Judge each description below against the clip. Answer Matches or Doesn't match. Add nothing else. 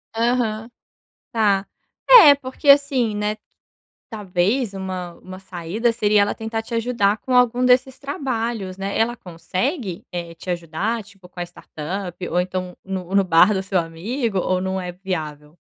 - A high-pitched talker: Matches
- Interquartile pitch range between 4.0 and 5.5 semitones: Matches